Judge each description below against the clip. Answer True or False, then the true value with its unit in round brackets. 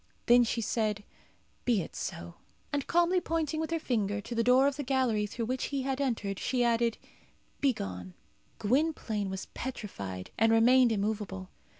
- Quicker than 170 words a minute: False (165 wpm)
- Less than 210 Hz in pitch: False (235 Hz)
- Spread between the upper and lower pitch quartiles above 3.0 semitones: True (4.4 semitones)